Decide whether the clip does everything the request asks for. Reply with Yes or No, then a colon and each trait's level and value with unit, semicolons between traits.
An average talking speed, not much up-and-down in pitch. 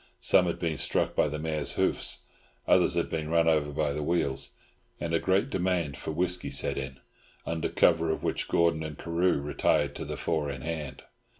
Yes: average, 195 wpm; narrow, 2.3 semitones